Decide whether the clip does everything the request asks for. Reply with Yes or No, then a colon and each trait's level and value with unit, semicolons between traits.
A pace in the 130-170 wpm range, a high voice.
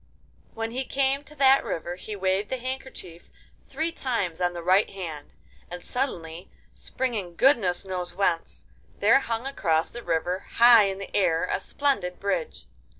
Yes: average, 155 wpm; high, 200 Hz